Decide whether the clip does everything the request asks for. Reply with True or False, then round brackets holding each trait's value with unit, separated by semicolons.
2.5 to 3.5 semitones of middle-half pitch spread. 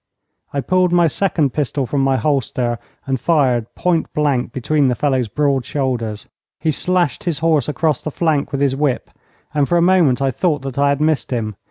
True (3.2 semitones)